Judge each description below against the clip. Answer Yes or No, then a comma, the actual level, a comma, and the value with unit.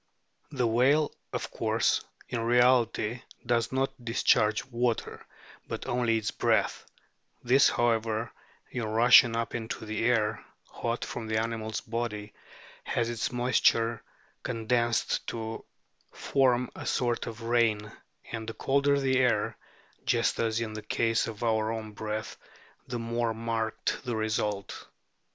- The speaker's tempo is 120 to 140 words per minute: Yes, slow, 135 wpm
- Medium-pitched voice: No, low, 115 Hz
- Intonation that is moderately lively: No, narrow, 1.6 semitones